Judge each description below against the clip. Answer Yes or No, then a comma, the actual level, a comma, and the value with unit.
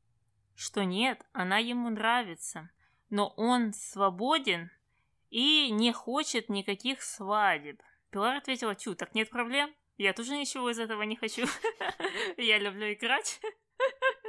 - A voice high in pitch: Yes, high, 230 Hz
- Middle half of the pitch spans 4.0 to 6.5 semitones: Yes, average, 4.7 semitones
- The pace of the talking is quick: No, average, 120 wpm